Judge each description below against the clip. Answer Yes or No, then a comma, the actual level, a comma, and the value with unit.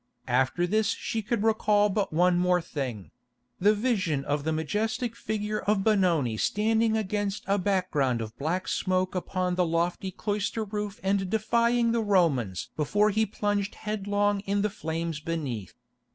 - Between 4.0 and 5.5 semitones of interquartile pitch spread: Yes, average, 4.6 semitones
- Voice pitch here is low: No, high, 195 Hz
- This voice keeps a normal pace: Yes, average, 150 wpm